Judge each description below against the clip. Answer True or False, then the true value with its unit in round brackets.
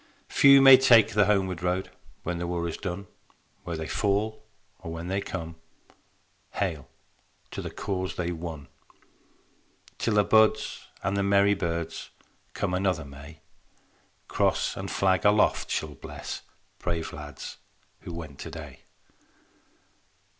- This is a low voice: True (90 Hz)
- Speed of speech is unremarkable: False (130 wpm)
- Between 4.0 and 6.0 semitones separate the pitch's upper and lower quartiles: False (3.4 semitones)